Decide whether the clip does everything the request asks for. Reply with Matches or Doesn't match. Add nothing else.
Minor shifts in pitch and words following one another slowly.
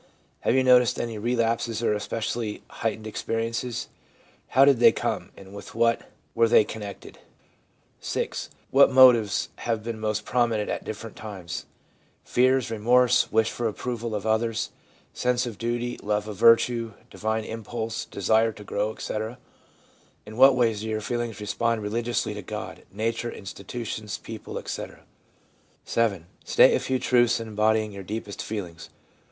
Doesn't match